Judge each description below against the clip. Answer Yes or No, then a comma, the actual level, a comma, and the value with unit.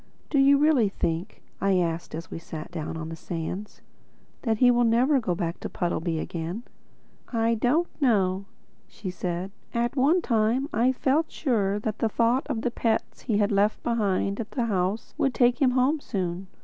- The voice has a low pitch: No, high, 220 Hz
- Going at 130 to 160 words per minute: No, average, 185 wpm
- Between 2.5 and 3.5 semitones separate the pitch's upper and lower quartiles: No, average, 5.3 semitones